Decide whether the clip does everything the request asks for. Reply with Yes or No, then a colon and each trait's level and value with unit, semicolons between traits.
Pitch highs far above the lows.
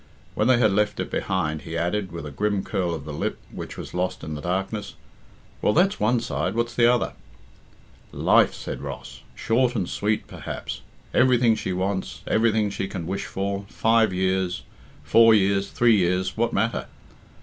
No: average, 3.6 semitones